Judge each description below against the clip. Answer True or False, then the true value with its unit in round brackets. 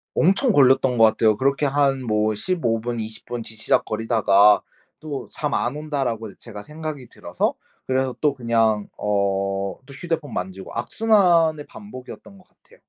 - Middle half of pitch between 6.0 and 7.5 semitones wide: False (5.5 semitones)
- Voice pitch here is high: False (130 Hz)